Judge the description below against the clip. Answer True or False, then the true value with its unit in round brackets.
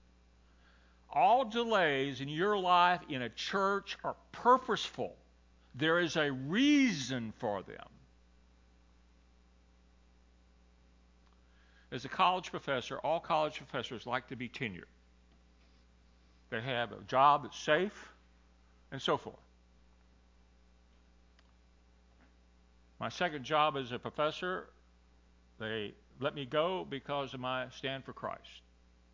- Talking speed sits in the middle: False (105 wpm)